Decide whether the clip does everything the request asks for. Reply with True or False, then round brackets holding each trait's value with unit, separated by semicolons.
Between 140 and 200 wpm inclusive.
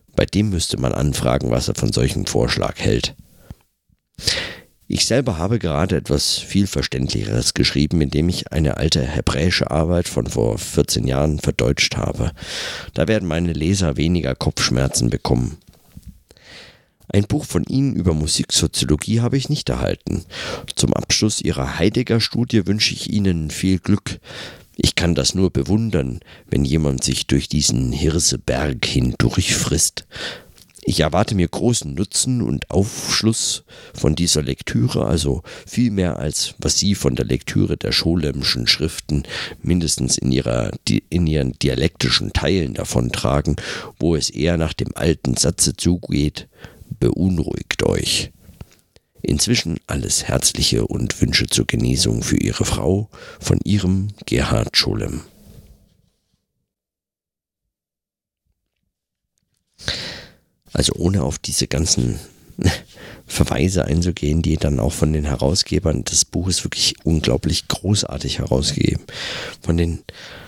False (125 wpm)